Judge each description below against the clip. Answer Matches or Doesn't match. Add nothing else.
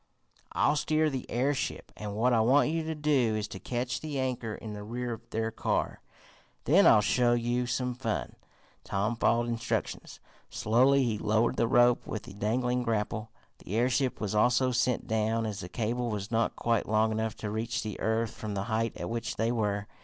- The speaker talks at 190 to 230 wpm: Matches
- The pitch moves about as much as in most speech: Doesn't match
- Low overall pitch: Matches